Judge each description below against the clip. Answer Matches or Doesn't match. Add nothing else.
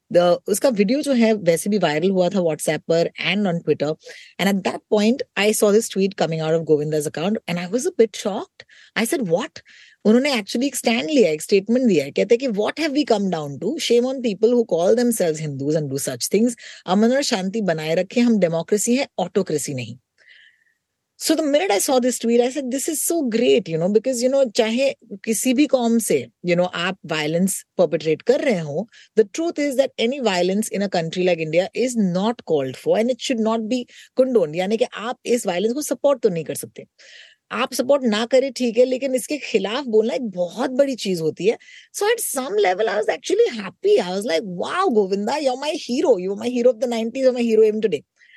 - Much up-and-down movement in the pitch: Matches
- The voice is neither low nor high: Doesn't match